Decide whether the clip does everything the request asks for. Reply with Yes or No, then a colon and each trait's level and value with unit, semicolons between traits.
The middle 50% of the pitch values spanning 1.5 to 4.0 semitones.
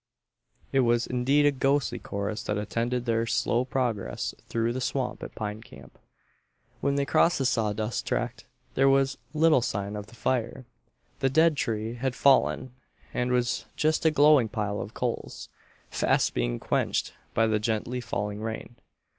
Yes: average, 3.7 semitones